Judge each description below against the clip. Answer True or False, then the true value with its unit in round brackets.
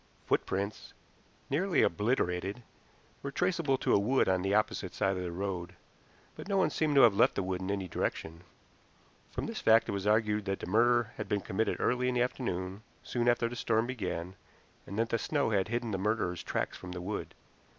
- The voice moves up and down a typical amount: True (4.4 semitones)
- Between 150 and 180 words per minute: False (200 wpm)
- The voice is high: False (105 Hz)